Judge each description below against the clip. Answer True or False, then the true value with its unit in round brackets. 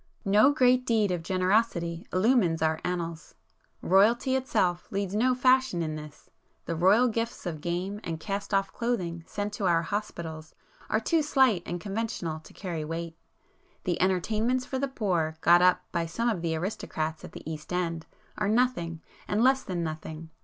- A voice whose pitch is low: False (185 Hz)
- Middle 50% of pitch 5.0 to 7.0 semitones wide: True (5.3 semitones)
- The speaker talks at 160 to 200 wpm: True (165 wpm)